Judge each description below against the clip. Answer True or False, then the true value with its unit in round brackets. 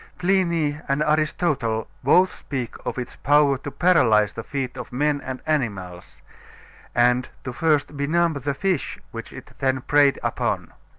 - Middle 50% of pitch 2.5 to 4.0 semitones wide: True (3.7 semitones)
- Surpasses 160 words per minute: False (150 wpm)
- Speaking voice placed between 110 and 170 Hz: True (140 Hz)